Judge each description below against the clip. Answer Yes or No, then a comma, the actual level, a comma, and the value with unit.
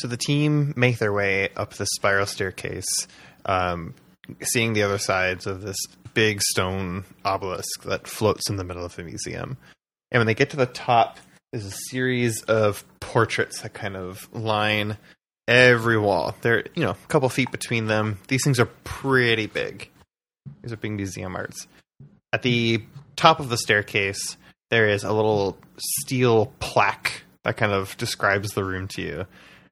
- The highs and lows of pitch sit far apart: No, average, 3.8 semitones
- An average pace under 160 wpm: No, average, 170 wpm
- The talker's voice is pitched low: Yes, low, 110 Hz